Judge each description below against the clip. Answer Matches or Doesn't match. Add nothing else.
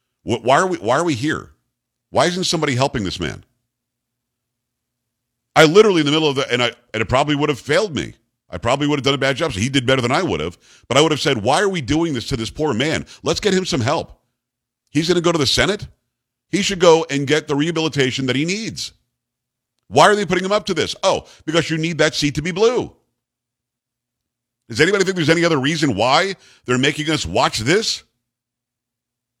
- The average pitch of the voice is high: Doesn't match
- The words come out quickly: Matches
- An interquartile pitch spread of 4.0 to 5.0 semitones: Matches